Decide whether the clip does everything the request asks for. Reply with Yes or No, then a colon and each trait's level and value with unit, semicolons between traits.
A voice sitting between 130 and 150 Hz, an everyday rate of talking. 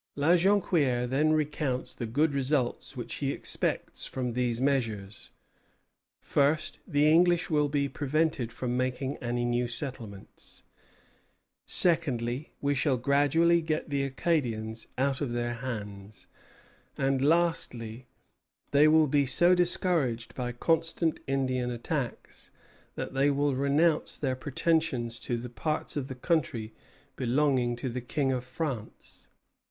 No: low, 135 Hz; slow, 130 wpm